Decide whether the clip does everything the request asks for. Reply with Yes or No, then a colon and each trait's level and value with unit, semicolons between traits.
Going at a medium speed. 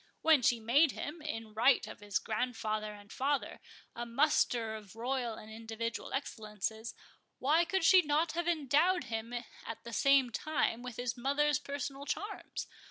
Yes: average, 160 wpm